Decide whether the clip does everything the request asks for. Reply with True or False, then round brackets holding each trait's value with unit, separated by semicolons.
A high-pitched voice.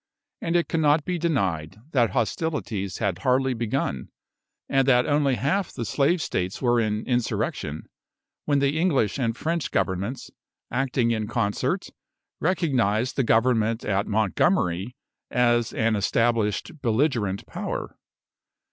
False (120 Hz)